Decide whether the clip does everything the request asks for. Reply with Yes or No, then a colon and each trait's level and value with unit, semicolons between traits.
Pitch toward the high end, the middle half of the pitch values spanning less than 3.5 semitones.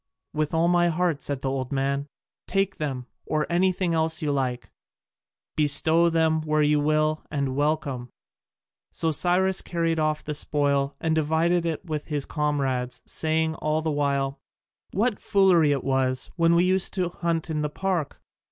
No: medium, 155 Hz; average, 2.9 semitones